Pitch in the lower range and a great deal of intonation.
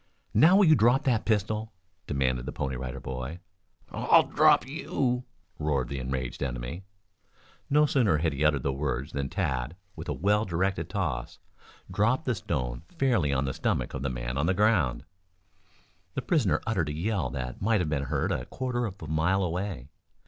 Yes: very low, 80 Hz; wide, 8.4 semitones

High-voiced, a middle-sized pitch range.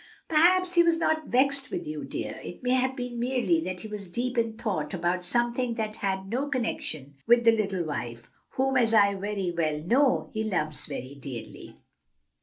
No: high, 230 Hz; wide, 6.2 semitones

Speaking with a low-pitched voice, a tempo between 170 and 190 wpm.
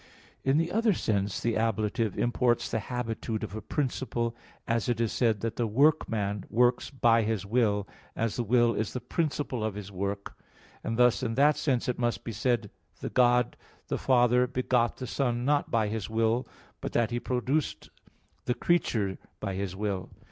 Yes: low, 115 Hz; average, 180 wpm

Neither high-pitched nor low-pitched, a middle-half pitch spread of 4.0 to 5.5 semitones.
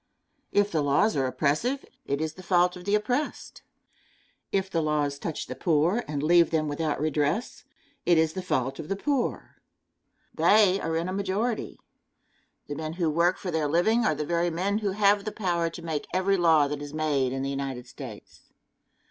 Yes: medium, 165 Hz; average, 4.7 semitones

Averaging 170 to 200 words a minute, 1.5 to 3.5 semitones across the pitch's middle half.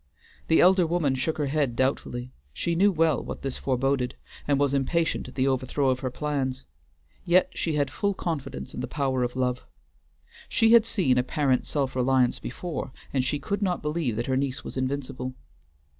No: average, 185 wpm; average, 4.0 semitones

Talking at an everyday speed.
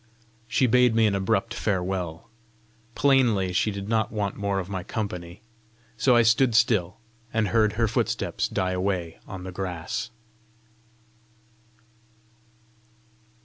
No: slow, 125 wpm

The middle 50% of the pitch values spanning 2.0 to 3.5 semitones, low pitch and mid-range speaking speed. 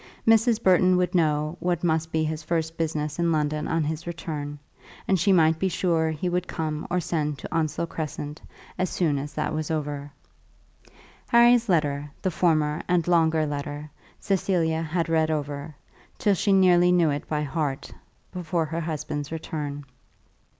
No: average, 2.7 semitones; medium, 160 Hz; average, 165 wpm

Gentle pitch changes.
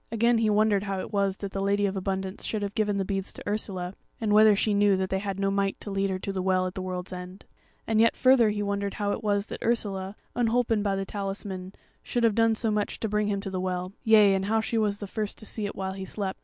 Yes: narrow, 1.9 semitones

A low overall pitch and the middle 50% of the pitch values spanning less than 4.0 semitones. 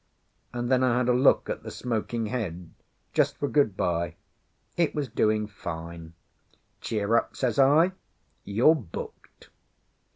No: low, 115 Hz; wide, 5.6 semitones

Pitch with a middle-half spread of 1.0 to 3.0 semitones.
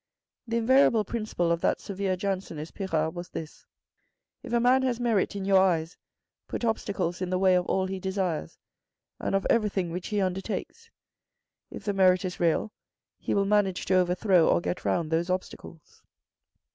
Yes: average, 2.7 semitones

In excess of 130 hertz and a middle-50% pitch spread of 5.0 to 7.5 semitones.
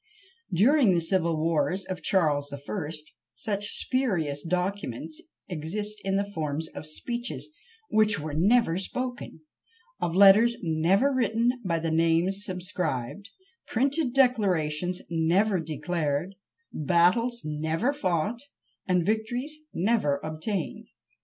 Yes: medium, 185 Hz; wide, 5.5 semitones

